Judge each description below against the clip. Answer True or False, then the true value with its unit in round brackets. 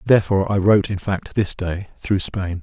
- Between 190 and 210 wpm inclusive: True (205 wpm)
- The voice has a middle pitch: False (95 Hz)